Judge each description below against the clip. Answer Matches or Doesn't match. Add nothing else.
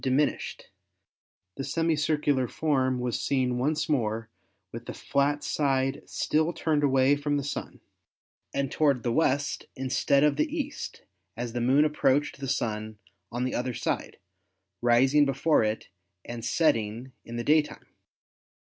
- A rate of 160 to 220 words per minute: Doesn't match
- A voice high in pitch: Doesn't match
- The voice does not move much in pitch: Doesn't match